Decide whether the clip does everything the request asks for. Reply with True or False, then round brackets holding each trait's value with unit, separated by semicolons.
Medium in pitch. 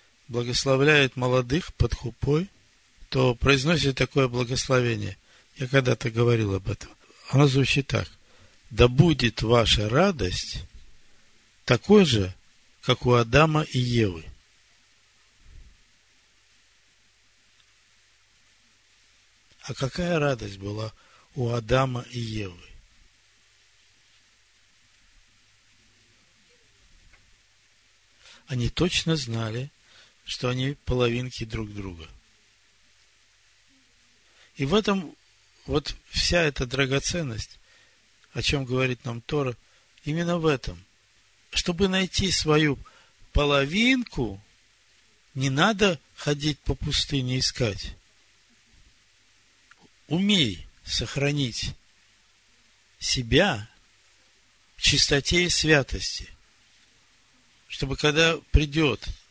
False (120 Hz)